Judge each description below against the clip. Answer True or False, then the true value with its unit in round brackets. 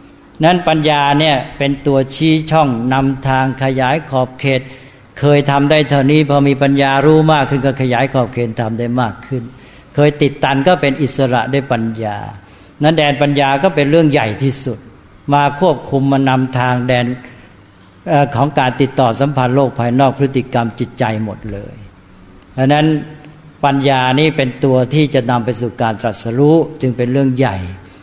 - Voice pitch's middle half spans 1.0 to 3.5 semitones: True (2.8 semitones)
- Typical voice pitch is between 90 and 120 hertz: False (135 Hz)